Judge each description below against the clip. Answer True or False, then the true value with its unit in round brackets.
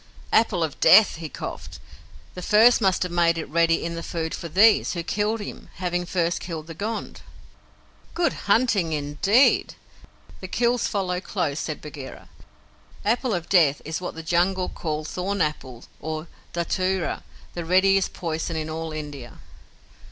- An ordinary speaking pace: True (155 wpm)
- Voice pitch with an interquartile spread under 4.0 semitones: True (3.4 semitones)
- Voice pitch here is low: False (175 Hz)